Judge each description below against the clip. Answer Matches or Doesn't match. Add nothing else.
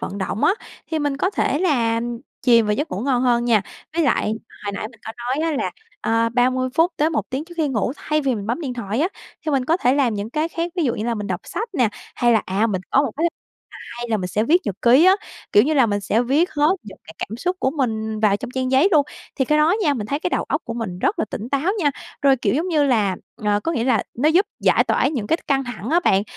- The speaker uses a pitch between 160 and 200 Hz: Doesn't match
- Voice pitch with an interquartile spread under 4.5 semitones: Doesn't match